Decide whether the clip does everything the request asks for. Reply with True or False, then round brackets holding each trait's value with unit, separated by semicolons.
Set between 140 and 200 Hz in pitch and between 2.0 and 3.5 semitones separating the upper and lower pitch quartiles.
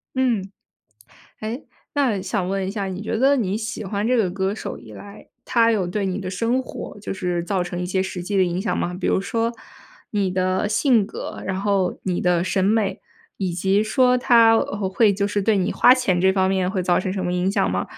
True (195 Hz; 2.9 semitones)